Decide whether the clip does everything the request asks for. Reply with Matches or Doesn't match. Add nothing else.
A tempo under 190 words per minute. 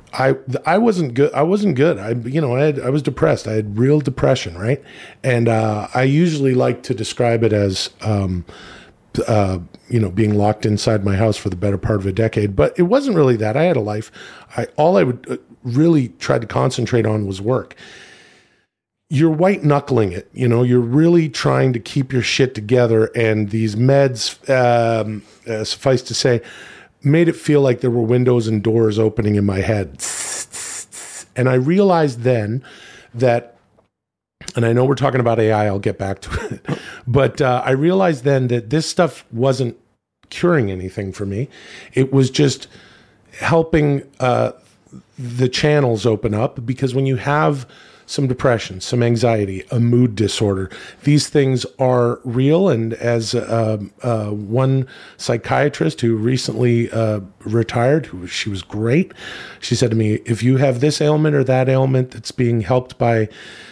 Matches